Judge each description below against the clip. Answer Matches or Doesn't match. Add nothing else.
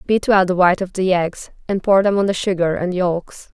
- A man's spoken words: Doesn't match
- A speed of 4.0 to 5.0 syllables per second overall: Doesn't match